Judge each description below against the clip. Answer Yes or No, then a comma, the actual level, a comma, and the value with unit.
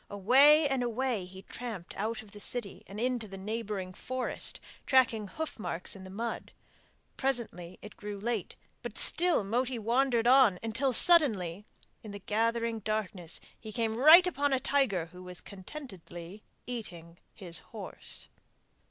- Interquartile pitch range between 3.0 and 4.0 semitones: No, average, 4.6 semitones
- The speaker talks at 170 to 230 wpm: No, average, 150 wpm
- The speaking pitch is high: Yes, high, 220 Hz